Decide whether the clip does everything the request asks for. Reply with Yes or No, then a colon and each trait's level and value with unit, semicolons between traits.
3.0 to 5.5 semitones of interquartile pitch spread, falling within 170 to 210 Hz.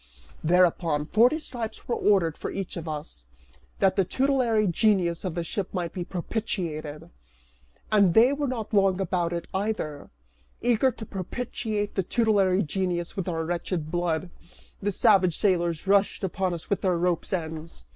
Yes: average, 3.8 semitones; medium, 185 Hz